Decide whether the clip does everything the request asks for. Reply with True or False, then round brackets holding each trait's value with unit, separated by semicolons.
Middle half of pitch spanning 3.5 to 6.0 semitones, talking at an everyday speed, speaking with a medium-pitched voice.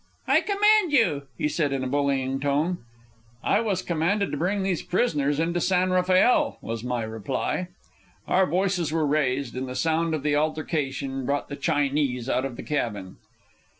True (5.1 semitones; 170 wpm; 150 Hz)